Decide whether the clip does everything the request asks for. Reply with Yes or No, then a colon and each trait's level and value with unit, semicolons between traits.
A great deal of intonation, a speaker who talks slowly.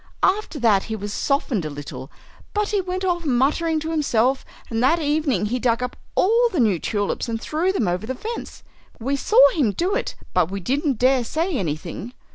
No: wide, 7.5 semitones; average, 200 wpm